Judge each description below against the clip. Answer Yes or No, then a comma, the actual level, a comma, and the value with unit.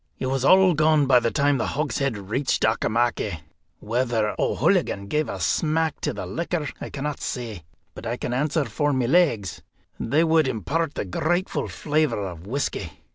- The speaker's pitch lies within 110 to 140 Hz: Yes, low, 135 Hz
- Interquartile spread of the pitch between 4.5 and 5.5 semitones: Yes, average, 5.2 semitones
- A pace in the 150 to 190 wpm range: Yes, average, 170 wpm